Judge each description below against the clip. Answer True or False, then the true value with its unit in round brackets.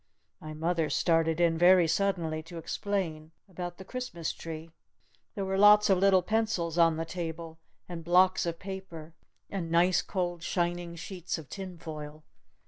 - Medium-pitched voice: True (175 Hz)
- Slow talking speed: False (155 wpm)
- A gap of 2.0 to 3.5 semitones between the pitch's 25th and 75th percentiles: True (2.5 semitones)